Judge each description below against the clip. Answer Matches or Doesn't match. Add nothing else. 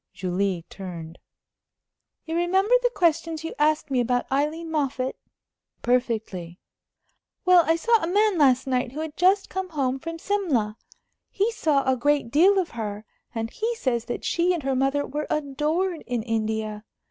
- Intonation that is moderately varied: Doesn't match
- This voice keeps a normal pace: Matches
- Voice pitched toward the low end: Doesn't match